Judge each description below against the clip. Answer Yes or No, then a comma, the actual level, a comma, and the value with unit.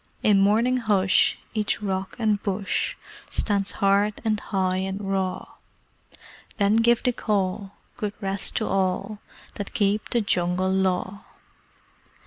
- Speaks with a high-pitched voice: Yes, high, 200 Hz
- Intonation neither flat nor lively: No, narrow, 1.9 semitones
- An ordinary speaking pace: No, slow, 125 wpm